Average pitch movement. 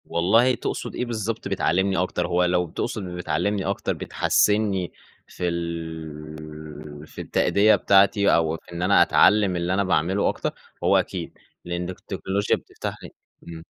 Yes: average, 3.2 semitones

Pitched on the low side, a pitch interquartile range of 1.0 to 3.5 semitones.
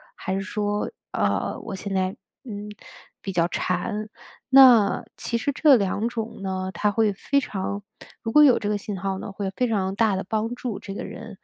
No: high, 205 Hz; average, 2.8 semitones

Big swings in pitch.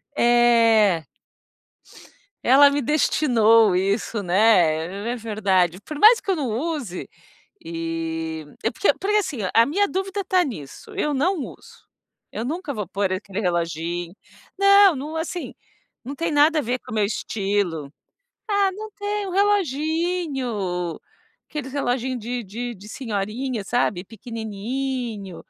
Yes: wide, 7.6 semitones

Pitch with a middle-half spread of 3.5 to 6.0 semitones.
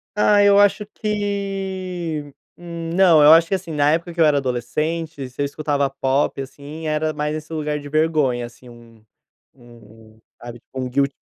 Yes: average, 3.9 semitones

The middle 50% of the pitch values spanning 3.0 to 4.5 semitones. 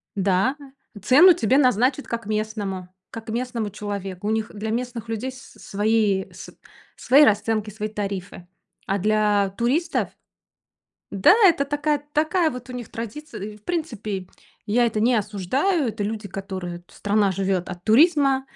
Yes: average, 4.0 semitones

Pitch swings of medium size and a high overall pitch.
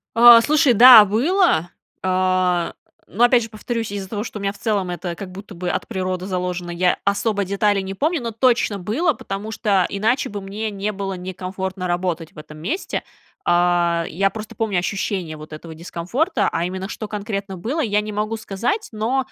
Yes: average, 3.4 semitones; high, 200 Hz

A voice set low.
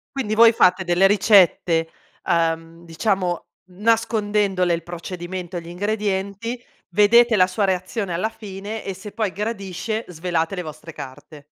No: high, 190 Hz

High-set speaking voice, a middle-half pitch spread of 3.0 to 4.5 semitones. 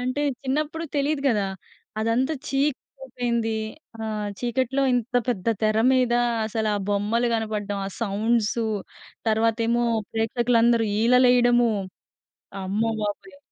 No: high, 235 Hz; narrow, 2.4 semitones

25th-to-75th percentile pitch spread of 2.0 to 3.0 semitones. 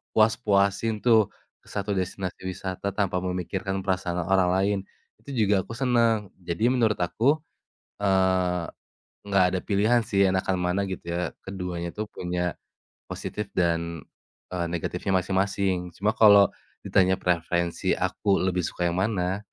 Yes: narrow, 2.4 semitones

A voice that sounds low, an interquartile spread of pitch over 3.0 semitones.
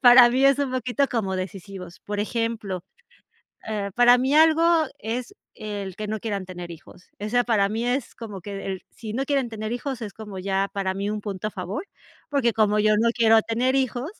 No: high, 220 Hz; average, 3.7 semitones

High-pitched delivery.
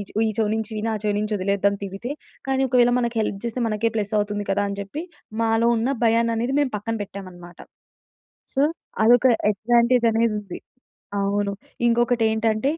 Yes: high, 220 Hz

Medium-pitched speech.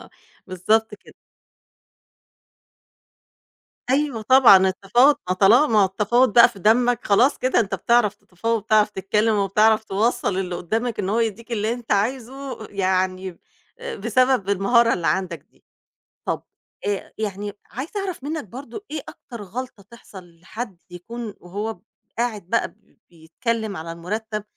No: high, 215 Hz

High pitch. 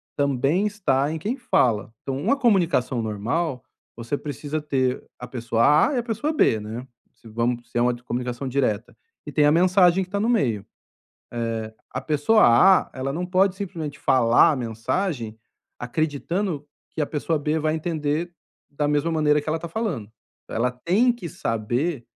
No: medium, 145 Hz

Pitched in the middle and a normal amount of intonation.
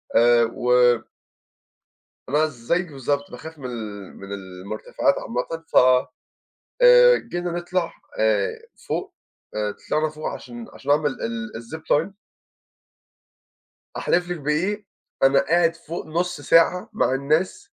No: medium, 150 Hz; wide, 6.6 semitones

